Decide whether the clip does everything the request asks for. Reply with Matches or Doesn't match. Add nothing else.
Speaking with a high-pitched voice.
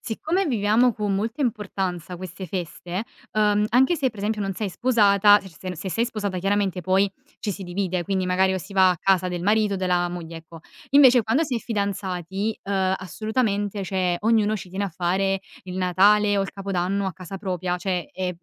Matches